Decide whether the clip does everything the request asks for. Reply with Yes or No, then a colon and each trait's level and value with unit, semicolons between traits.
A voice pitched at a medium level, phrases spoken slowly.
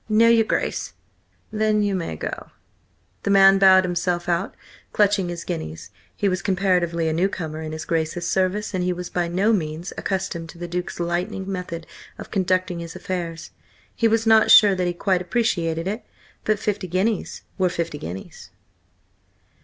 No: medium, 180 Hz; average, 170 wpm